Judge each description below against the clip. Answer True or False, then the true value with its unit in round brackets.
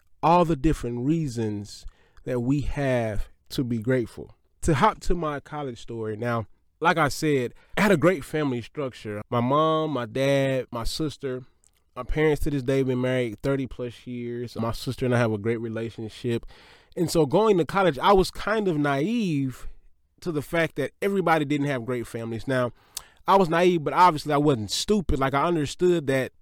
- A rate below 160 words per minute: False (190 wpm)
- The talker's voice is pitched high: False (135 Hz)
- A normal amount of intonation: True (4.9 semitones)